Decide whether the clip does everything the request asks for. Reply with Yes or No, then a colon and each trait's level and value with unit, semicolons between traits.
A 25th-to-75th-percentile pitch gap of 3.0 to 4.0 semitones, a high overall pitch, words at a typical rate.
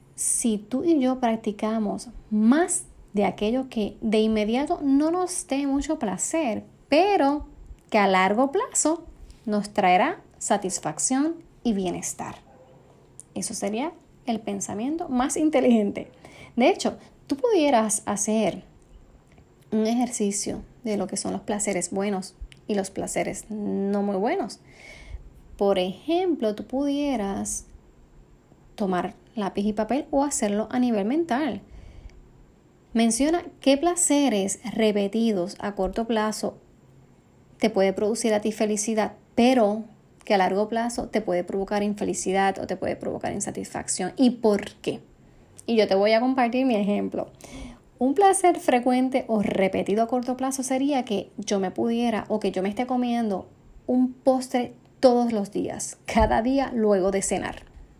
No: average, 4.5 semitones; high, 220 Hz; average, 135 wpm